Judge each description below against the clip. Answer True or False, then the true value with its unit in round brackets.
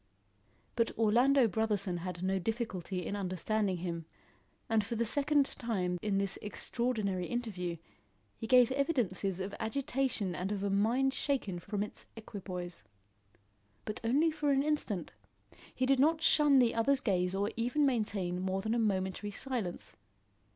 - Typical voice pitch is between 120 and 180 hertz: False (215 Hz)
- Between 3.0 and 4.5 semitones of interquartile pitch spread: False (5.1 semitones)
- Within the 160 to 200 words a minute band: False (150 wpm)